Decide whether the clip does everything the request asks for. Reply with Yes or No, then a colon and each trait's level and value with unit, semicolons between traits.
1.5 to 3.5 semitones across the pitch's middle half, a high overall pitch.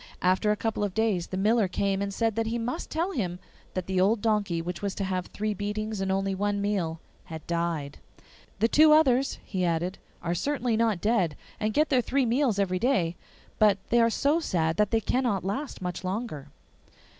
No: average, 4.0 semitones; high, 205 Hz